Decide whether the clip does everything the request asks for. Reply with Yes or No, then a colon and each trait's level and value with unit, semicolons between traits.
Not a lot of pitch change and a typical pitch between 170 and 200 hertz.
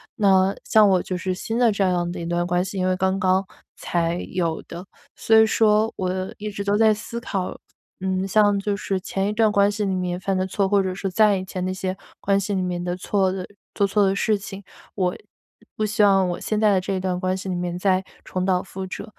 Yes: narrow, 1.8 semitones; high, 190 Hz